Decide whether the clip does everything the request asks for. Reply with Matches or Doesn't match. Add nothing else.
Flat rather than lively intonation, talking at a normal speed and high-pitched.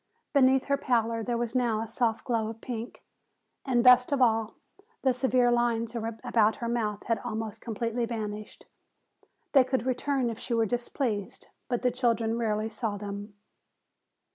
Matches